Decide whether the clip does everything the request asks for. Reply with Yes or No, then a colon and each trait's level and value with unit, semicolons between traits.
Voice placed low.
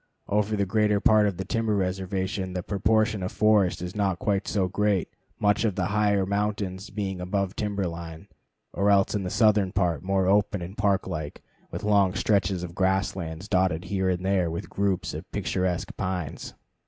Yes: very low, 95 Hz